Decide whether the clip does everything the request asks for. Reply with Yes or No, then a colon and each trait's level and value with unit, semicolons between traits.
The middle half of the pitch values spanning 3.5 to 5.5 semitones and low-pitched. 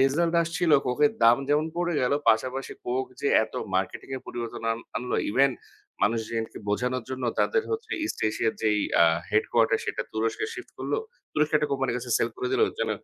Yes: average, 5.0 semitones; low, 130 Hz